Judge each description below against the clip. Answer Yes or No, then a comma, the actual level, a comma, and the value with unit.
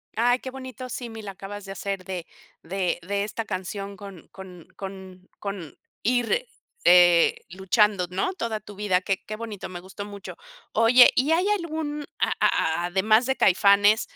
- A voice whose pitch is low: No, high, 200 Hz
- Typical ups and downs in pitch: Yes, average, 3.6 semitones